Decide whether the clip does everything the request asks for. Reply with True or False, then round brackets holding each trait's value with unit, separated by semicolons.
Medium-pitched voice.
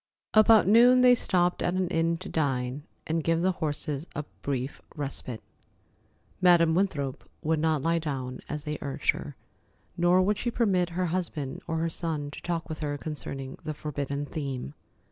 True (160 Hz)